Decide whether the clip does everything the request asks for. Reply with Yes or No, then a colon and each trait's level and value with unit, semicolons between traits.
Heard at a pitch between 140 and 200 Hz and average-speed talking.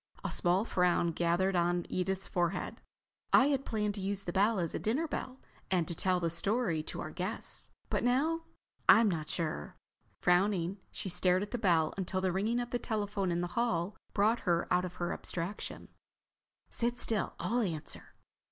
Yes: high, 190 Hz; average, 180 wpm